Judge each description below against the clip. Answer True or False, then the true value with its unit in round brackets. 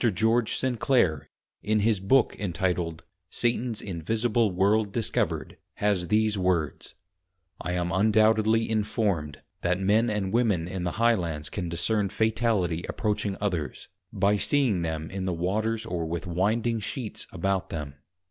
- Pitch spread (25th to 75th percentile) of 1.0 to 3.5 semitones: False (4.1 semitones)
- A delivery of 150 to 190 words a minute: False (140 wpm)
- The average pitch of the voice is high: False (100 Hz)